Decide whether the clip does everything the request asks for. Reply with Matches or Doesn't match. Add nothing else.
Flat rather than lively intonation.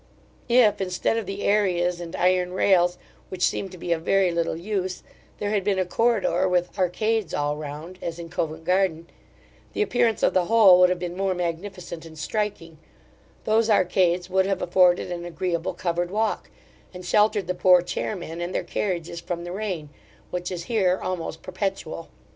Matches